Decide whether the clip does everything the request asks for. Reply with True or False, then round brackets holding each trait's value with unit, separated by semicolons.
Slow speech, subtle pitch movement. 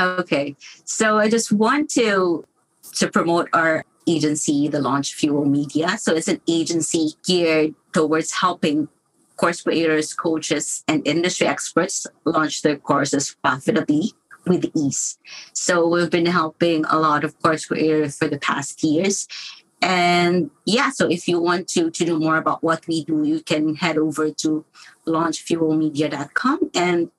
False (150 wpm; 2.2 semitones)